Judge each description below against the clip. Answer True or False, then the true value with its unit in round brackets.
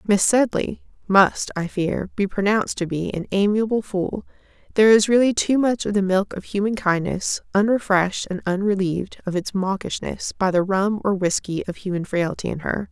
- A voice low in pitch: False (195 Hz)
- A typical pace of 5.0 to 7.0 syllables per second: True (5.1 syllables/s)